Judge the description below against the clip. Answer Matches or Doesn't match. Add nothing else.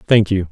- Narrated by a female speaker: Doesn't match